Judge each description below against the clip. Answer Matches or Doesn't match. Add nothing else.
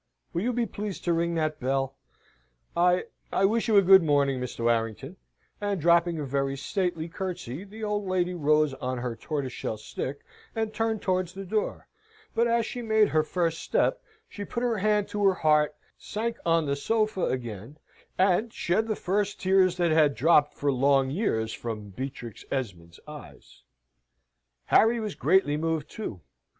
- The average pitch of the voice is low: Doesn't match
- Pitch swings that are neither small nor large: Doesn't match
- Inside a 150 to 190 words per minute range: Matches